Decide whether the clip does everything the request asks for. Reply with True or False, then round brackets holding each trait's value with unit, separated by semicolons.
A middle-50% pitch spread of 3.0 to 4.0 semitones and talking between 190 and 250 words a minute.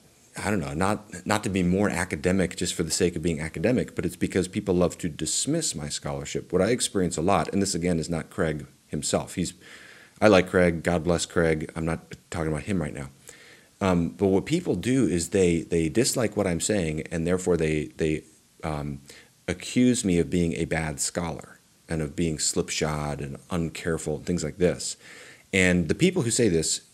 True (3.3 semitones; 205 wpm)